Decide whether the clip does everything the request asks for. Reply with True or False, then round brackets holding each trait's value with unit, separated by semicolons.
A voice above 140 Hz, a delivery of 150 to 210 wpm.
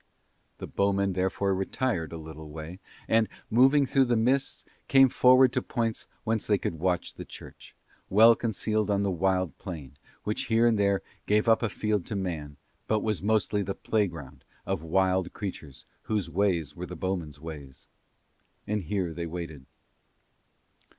False (95 Hz; 160 wpm)